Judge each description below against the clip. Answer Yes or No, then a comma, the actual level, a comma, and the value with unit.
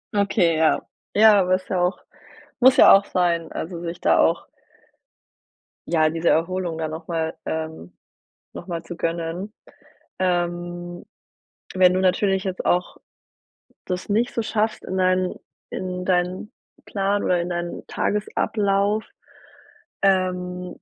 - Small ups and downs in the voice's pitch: Yes, narrow, 2.1 semitones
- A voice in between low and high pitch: Yes, medium, 180 Hz